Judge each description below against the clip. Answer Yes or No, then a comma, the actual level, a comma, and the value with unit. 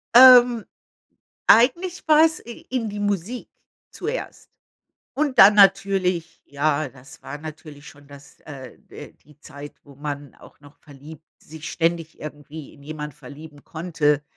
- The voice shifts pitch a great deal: Yes, wide, 6.0 semitones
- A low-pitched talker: No, medium, 155 Hz